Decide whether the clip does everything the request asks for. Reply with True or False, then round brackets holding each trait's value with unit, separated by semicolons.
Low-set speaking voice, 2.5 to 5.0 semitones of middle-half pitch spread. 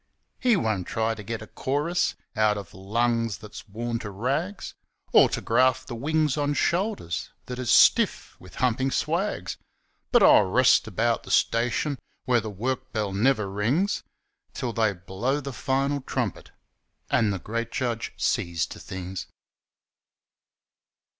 True (120 Hz; 4.3 semitones)